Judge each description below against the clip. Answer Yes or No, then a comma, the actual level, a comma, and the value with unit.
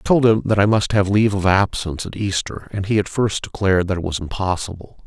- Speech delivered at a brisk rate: Yes, fast, 250 wpm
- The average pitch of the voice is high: No, low, 100 Hz